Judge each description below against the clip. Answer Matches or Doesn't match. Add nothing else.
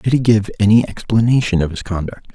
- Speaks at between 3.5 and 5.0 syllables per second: Doesn't match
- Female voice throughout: Doesn't match